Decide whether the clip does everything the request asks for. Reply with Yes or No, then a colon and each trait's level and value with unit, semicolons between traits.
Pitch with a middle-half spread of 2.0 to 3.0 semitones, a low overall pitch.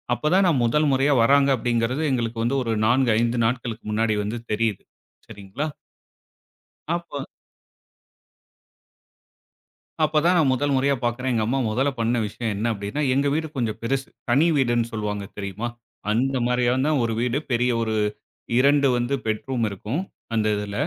No: average, 3.4 semitones; low, 120 Hz